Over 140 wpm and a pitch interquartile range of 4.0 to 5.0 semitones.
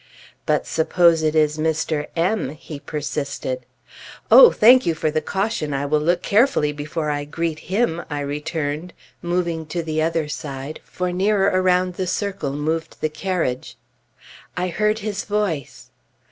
No: average, 155 wpm; average, 3.6 semitones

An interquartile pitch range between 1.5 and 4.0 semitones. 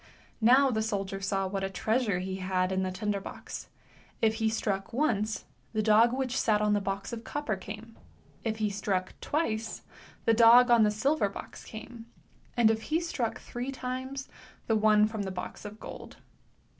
Yes: average, 3.2 semitones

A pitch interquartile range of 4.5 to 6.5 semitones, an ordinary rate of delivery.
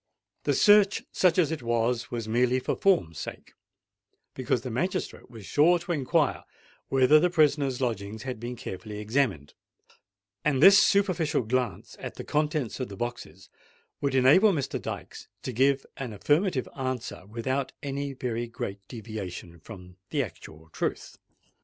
Yes: average, 4.9 semitones; average, 150 wpm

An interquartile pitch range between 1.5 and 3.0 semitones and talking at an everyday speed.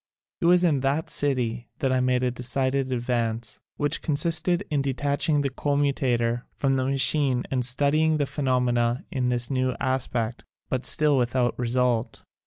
Yes: narrow, 2.6 semitones; average, 160 wpm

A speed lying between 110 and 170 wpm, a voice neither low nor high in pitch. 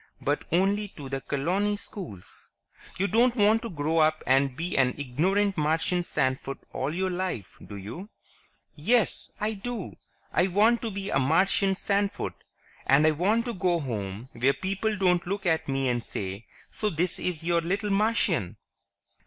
Yes: average, 165 wpm; medium, 175 Hz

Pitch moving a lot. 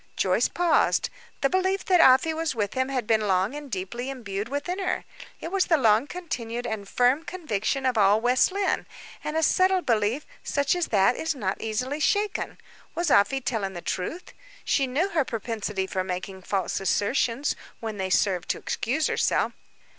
Yes: wide, 7.3 semitones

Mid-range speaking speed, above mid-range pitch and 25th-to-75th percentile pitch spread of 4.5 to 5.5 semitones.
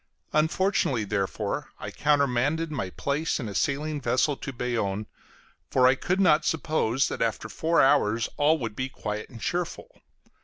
No: average, 155 wpm; low, 135 Hz; average, 5.2 semitones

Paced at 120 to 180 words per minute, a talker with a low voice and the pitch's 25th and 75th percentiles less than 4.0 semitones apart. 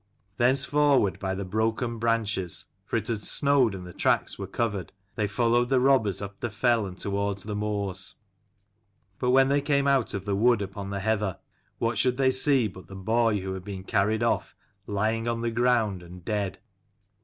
No: average, 190 wpm; low, 110 Hz; average, 3.6 semitones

